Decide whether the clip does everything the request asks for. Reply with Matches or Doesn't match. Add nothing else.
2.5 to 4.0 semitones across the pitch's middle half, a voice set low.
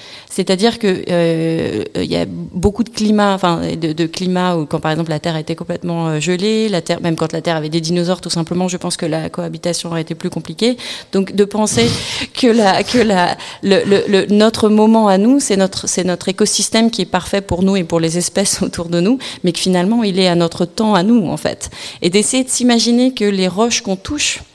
Doesn't match